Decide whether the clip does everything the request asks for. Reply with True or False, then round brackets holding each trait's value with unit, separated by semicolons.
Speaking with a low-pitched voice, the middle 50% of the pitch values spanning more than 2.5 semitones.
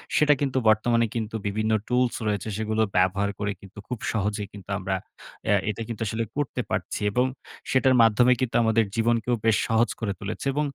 True (110 Hz; 2.9 semitones)